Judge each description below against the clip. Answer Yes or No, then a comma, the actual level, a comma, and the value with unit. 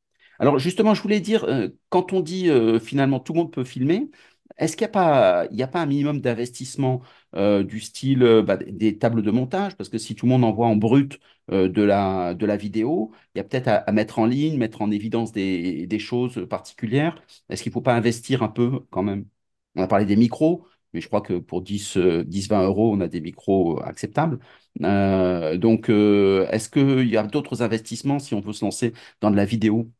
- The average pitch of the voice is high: No, low, 115 Hz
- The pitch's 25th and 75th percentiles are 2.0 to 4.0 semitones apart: No, average, 4.8 semitones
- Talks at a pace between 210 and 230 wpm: Yes, fast, 220 wpm